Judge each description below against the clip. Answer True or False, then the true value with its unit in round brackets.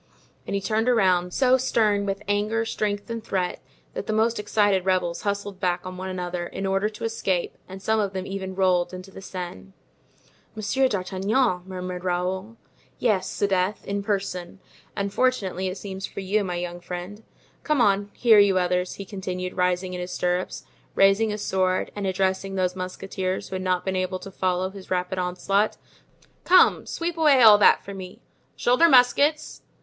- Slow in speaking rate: False (175 wpm)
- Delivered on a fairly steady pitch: True (2.3 semitones)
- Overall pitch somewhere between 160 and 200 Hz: True (190 Hz)